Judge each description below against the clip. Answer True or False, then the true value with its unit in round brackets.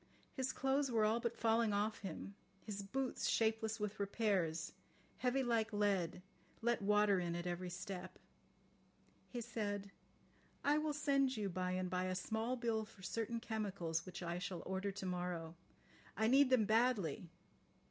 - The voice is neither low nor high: False (210 Hz)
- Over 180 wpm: False (160 wpm)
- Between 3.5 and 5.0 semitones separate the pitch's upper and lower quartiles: True (4.1 semitones)